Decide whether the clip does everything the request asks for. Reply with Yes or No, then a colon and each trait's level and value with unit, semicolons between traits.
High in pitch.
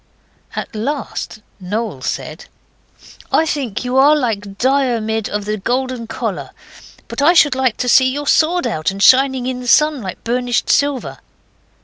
Yes: very high, 250 Hz